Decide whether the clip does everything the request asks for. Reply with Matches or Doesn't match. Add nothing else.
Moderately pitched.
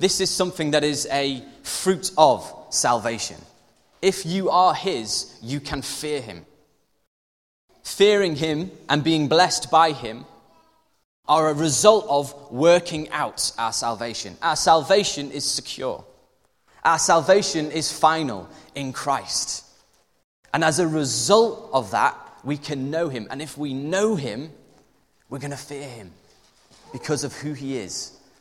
Matches